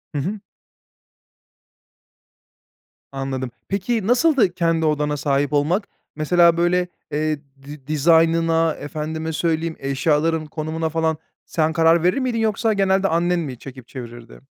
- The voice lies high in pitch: No, medium, 160 Hz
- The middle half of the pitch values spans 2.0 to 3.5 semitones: Yes, average, 3.0 semitones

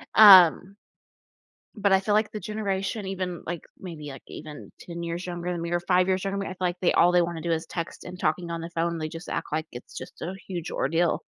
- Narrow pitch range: Yes, narrow, 2.2 semitones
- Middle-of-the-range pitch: Yes, medium, 175 Hz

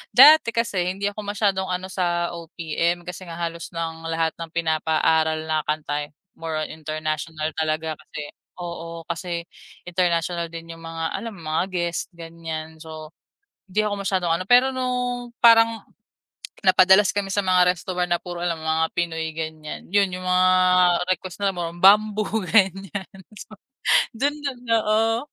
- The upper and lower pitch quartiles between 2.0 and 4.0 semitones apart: Yes, average, 3.5 semitones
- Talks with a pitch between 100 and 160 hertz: No, medium, 175 Hz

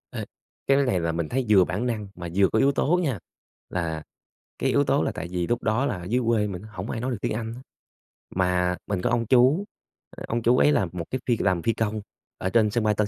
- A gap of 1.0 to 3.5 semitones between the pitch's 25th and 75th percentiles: No, average, 5.2 semitones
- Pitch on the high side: No, low, 110 Hz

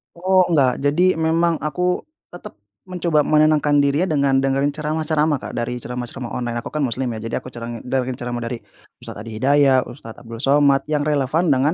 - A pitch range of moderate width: Yes, average, 3.9 semitones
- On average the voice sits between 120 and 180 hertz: Yes, medium, 140 Hz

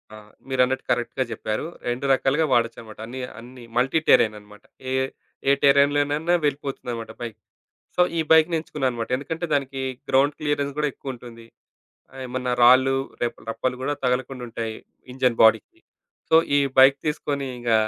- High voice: No, low, 130 Hz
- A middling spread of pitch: Yes, average, 3.0 semitones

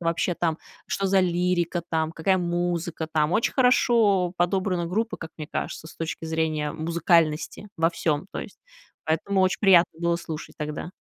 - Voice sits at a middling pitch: Yes, medium, 170 Hz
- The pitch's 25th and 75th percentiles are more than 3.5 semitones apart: No, narrow, 2.4 semitones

